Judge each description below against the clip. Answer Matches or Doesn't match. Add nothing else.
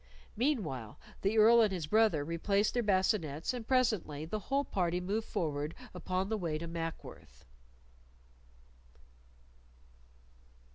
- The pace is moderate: Doesn't match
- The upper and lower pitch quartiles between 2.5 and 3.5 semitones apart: Doesn't match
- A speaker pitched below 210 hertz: Matches